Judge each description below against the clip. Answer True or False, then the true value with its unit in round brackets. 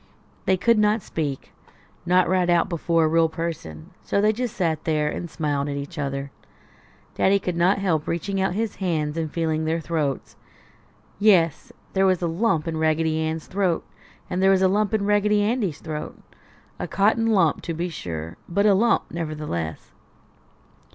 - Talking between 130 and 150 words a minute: False (175 wpm)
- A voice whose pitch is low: False (170 Hz)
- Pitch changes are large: False (3.9 semitones)